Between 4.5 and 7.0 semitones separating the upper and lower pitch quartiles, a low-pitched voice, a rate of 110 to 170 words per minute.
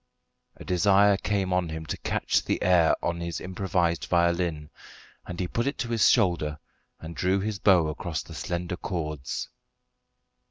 No: narrow, 2.5 semitones; very low, 90 Hz; average, 160 wpm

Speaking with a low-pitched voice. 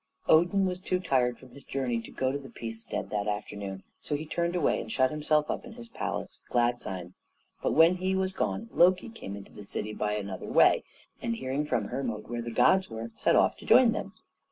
Yes: low, 130 Hz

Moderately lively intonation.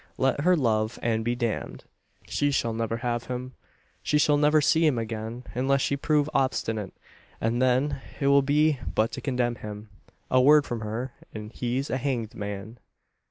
Yes: average, 3.7 semitones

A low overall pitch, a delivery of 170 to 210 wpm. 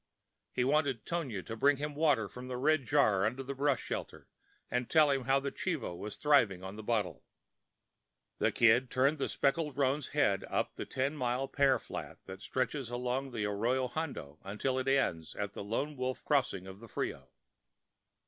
Yes: low, 130 Hz; average, 185 wpm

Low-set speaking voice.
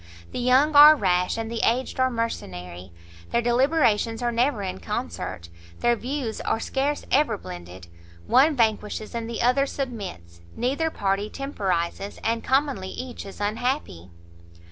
No: high, 230 Hz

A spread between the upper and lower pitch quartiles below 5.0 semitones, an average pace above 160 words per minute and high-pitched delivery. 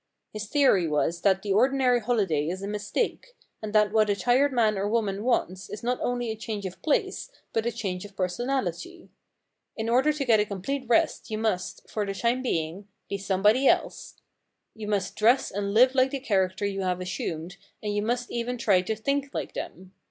Yes: average, 4.1 semitones; average, 200 wpm; high, 215 Hz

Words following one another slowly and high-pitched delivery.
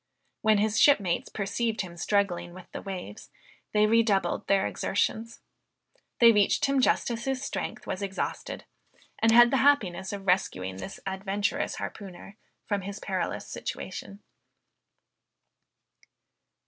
Yes: slow, 125 wpm; high, 200 Hz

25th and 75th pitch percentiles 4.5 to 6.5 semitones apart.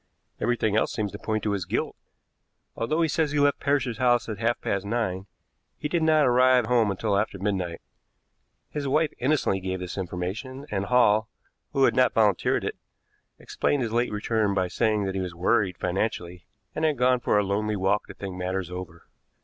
Yes: average, 4.8 semitones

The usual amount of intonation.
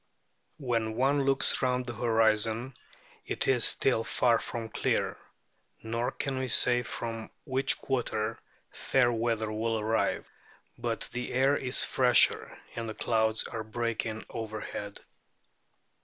No: narrow, 2.2 semitones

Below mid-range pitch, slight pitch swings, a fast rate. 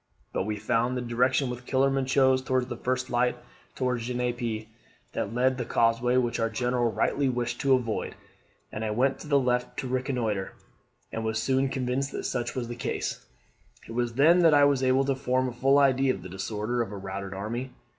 Yes: low, 125 Hz; narrow, 2.2 semitones; fast, 210 wpm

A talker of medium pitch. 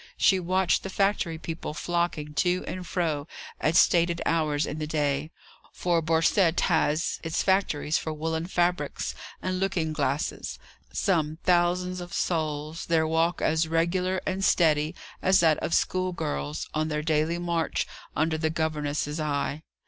Yes: medium, 165 Hz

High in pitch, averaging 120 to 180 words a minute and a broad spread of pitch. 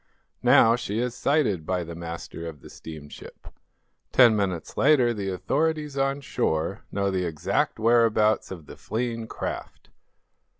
No: low, 105 Hz; average, 140 wpm; wide, 6.3 semitones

